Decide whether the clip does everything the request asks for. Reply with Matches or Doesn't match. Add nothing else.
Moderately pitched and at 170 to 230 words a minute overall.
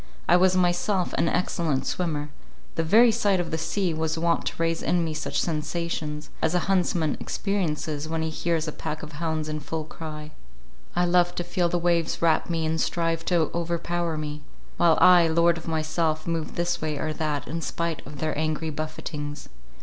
Matches